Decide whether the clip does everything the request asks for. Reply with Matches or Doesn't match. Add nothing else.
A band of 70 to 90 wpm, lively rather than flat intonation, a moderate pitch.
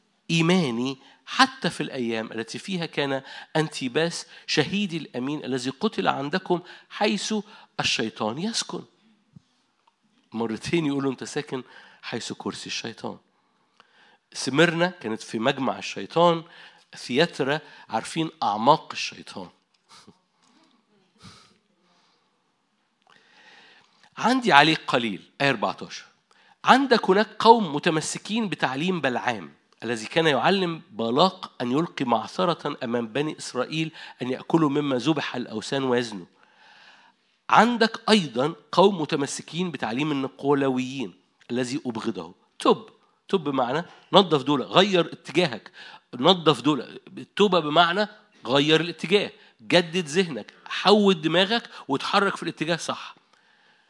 Doesn't match